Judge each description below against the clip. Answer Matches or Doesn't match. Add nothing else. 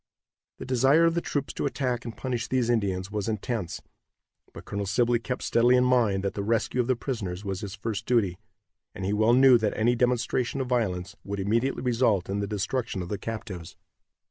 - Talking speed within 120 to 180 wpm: Doesn't match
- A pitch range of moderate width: Matches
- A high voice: Doesn't match